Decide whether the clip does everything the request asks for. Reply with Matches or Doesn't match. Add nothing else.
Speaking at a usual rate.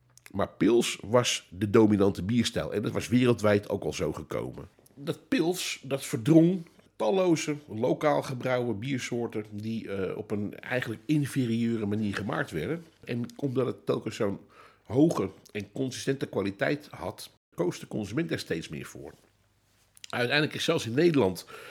Matches